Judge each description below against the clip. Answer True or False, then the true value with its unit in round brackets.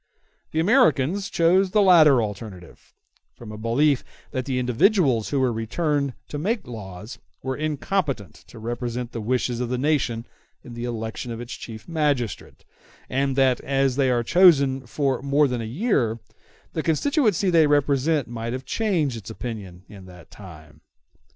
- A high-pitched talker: False (130 Hz)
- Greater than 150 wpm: True (165 wpm)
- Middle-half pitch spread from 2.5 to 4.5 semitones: False (4.9 semitones)